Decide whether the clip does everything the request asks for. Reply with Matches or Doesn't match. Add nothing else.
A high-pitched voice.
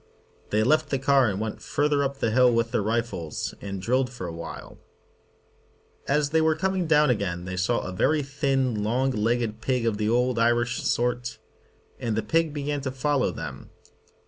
Doesn't match